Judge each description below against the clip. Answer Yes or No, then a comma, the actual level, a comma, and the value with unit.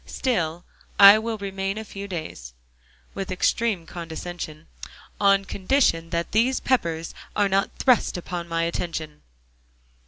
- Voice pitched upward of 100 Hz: Yes, medium, 185 Hz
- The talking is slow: Yes, slow, 125 wpm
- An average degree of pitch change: Yes, average, 3.6 semitones